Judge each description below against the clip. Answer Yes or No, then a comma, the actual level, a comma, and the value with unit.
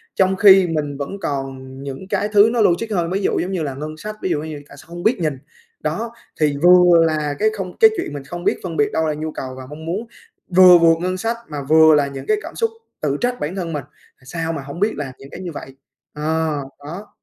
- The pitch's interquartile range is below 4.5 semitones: Yes, average, 4.1 semitones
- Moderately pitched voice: Yes, medium, 160 Hz